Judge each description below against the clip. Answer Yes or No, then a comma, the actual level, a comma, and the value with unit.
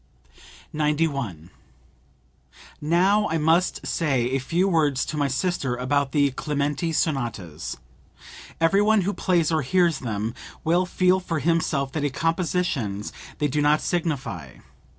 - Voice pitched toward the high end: No, medium, 150 Hz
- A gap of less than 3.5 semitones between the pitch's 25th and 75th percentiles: No, average, 4.2 semitones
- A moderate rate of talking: No, slow, 130 wpm